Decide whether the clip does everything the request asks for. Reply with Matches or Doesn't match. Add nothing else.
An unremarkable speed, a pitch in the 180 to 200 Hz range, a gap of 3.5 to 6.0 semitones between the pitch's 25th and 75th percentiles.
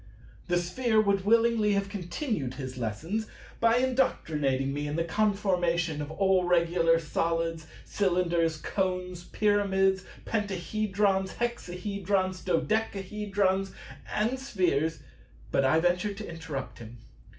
Doesn't match